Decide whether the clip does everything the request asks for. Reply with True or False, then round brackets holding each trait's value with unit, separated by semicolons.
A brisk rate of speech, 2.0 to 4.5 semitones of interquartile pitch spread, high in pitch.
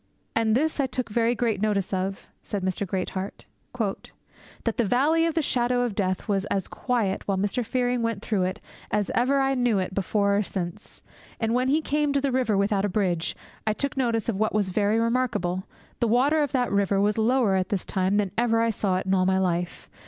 True (220 wpm; 4.2 semitones; 215 Hz)